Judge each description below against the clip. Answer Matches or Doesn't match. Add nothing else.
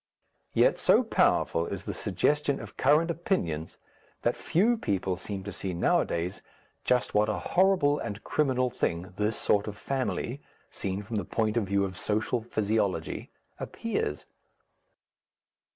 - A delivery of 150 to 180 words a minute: Doesn't match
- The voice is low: Matches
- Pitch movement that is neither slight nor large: Doesn't match